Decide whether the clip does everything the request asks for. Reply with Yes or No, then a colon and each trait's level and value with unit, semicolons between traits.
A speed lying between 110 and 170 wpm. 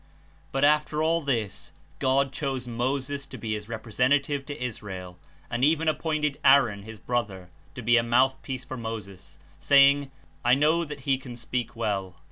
Yes: average, 165 wpm